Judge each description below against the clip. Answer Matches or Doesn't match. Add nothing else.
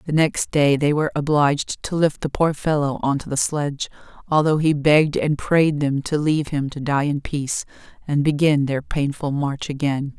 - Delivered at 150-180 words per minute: Doesn't match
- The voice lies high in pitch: Doesn't match